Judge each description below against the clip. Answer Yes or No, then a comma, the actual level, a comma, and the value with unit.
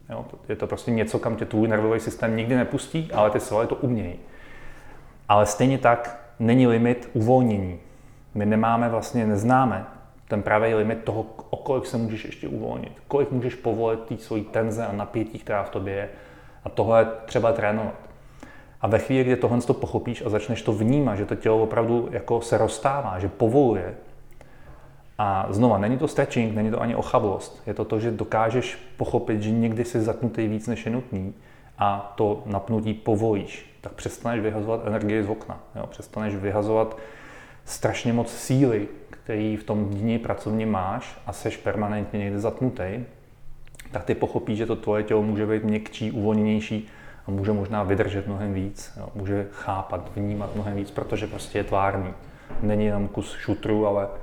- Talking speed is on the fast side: Yes, fast, 175 wpm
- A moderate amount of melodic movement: No, narrow, 2.2 semitones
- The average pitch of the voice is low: Yes, low, 110 Hz